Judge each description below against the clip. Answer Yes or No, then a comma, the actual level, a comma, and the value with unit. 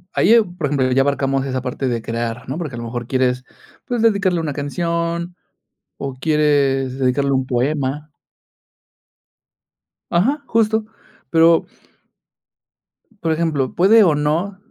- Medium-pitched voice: Yes, medium, 145 Hz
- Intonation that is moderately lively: Yes, average, 4.6 semitones